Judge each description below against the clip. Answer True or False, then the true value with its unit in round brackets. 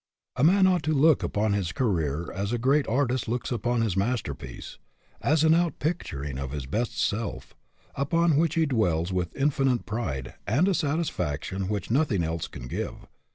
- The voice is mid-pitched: False (115 Hz)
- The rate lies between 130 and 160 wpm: False (170 wpm)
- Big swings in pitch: True (8.8 semitones)